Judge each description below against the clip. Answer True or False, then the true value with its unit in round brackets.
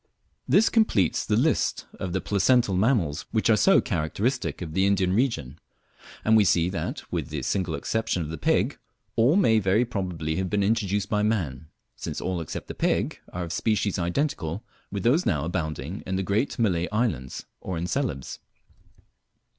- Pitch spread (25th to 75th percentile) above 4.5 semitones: True (5.0 semitones)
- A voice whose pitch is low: True (95 Hz)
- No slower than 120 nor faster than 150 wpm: False (175 wpm)